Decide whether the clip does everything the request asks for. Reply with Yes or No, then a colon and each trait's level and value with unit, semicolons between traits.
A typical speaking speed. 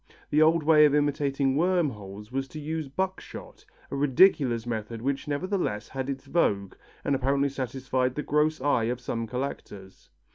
Yes: average, 160 wpm